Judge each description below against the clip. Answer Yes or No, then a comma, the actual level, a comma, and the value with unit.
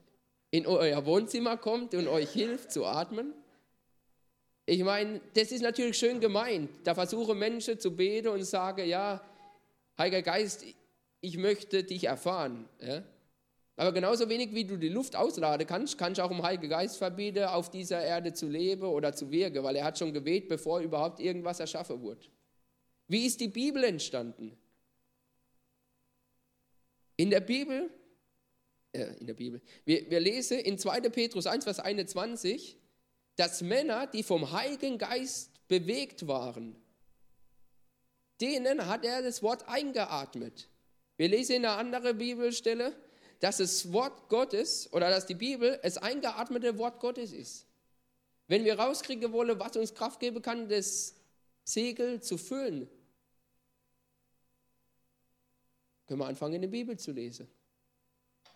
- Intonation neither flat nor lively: No, wide, 5.7 semitones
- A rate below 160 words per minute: Yes, average, 140 wpm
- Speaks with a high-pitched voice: Yes, high, 195 Hz